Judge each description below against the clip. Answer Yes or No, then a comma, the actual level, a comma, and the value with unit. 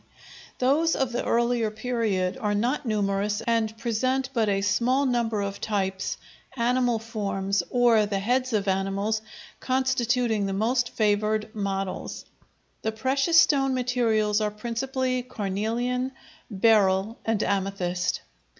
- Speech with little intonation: No, average, 3.5 semitones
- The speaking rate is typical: No, slow, 125 wpm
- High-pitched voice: Yes, high, 220 Hz